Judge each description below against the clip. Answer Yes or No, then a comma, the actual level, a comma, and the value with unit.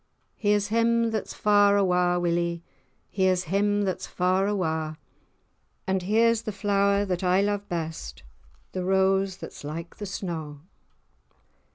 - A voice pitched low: No, high, 190 Hz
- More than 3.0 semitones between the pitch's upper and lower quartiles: No, narrow, 2.5 semitones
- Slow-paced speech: Yes, slow, 130 wpm